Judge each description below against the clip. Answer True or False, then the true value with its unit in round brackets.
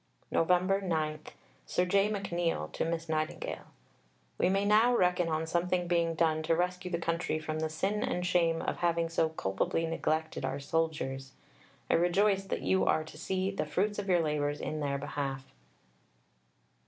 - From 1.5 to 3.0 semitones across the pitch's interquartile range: True (2.6 semitones)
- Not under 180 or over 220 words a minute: False (165 wpm)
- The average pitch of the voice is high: False (165 Hz)